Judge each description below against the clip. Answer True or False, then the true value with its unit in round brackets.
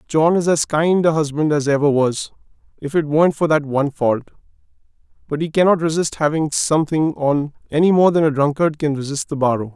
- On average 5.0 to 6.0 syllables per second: True (5.7 syllables/s)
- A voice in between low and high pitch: True (150 Hz)